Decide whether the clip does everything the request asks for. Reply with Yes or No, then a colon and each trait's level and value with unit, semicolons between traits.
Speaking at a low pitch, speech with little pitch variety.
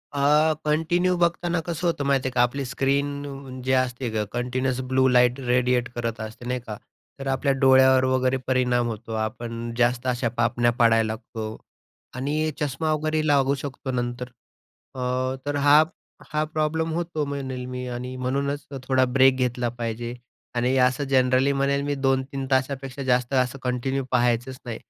Yes: low, 130 Hz; narrow, 2.3 semitones